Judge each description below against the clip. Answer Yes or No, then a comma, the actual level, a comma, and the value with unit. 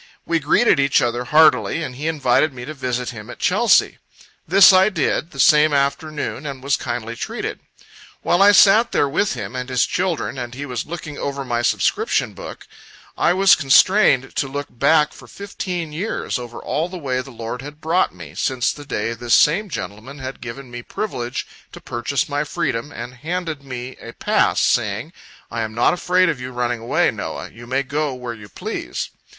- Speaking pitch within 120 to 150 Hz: Yes, medium, 140 Hz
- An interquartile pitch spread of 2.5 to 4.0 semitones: No, average, 4.5 semitones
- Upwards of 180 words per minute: Yes, average, 190 wpm